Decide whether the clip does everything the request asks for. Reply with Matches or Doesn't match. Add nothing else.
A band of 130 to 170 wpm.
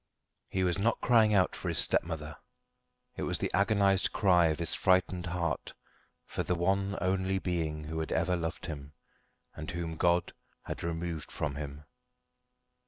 Matches